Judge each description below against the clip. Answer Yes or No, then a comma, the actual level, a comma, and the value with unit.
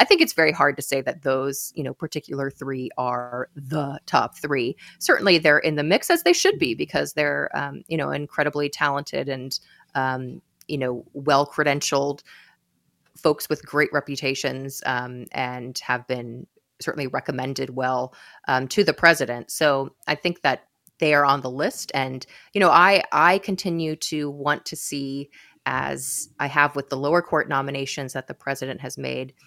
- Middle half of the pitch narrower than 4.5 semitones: Yes, narrow, 2.6 semitones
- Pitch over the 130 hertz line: Yes, medium, 140 Hz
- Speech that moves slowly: No, average, 175 wpm